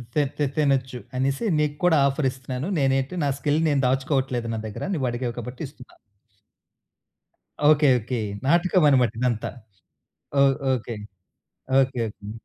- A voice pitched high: No, low, 135 Hz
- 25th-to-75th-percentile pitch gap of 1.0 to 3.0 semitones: Yes, average, 2.7 semitones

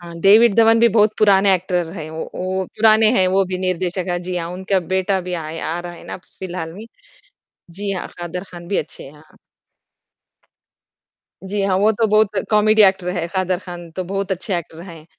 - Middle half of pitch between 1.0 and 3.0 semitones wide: Yes, narrow, 2.6 semitones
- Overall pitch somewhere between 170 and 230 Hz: Yes, medium, 185 Hz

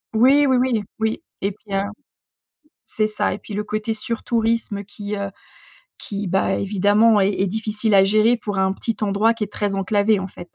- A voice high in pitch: Yes, high, 210 Hz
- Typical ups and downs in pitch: No, narrow, 1.9 semitones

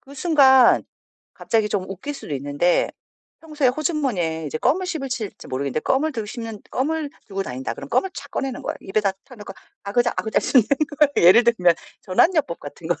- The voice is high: Yes, high, 230 Hz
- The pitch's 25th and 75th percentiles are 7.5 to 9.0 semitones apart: Yes, wide, 7.8 semitones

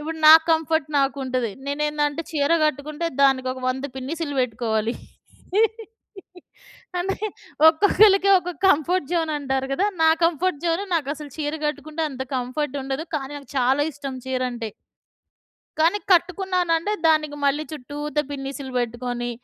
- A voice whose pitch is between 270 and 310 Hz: Yes, very high, 290 Hz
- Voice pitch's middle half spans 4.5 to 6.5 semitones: No, average, 3.5 semitones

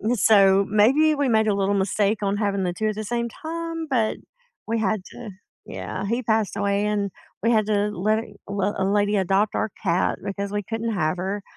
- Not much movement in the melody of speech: Yes, narrow, 2.0 semitones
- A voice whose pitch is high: Yes, high, 205 Hz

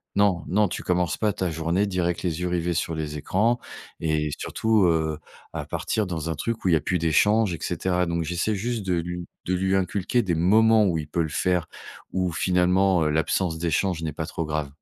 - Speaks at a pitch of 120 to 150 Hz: No, very low, 90 Hz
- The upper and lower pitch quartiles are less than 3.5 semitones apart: Yes, average, 2.9 semitones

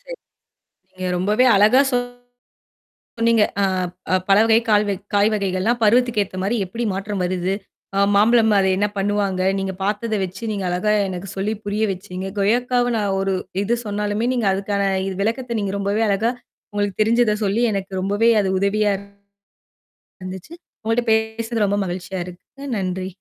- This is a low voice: No, high, 205 Hz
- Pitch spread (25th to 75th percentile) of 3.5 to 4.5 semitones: No, average, 2.7 semitones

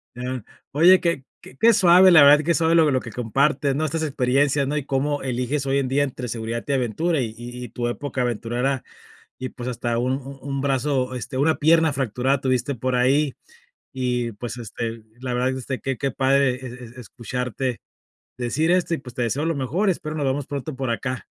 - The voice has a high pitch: No, low, 130 Hz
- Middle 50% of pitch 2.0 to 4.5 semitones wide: Yes, average, 2.8 semitones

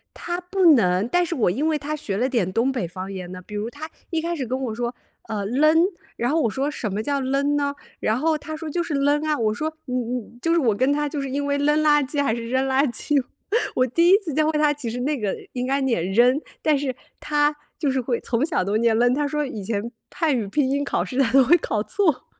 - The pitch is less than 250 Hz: No, very high, 270 Hz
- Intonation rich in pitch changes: No, average, 4.3 semitones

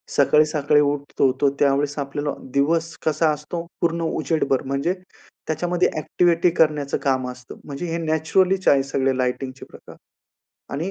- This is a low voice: No, medium, 150 Hz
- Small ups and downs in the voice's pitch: No, average, 3.0 semitones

